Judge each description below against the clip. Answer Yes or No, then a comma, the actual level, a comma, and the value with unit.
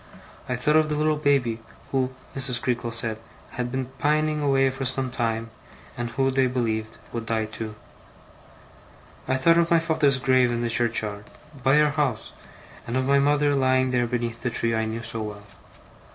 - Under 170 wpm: No, average, 180 wpm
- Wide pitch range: No, average, 3.2 semitones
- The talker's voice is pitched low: Yes, low, 130 Hz